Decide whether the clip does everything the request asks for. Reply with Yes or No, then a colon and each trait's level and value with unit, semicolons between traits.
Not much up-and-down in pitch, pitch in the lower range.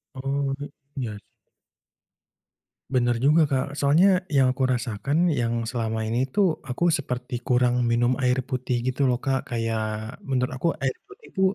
Yes: narrow, 2.1 semitones; low, 130 Hz